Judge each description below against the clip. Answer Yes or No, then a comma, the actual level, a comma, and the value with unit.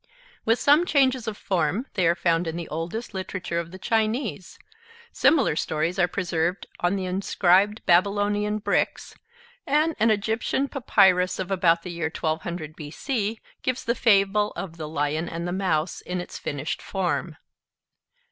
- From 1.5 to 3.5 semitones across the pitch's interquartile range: No, average, 4.3 semitones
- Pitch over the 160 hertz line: Yes, medium, 185 Hz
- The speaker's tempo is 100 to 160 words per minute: Yes, average, 155 wpm